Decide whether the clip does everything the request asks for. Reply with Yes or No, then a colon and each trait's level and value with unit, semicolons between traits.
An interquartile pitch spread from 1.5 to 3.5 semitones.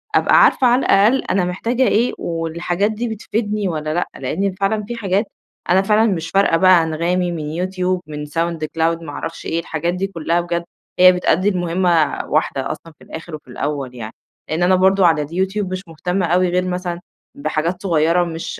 Yes: average, 2.9 semitones